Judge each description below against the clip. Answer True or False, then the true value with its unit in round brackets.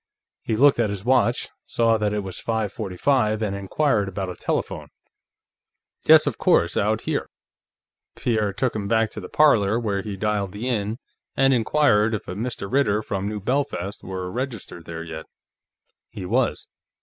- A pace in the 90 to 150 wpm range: False (175 wpm)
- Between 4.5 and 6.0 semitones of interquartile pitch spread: False (3.3 semitones)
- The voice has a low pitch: True (105 Hz)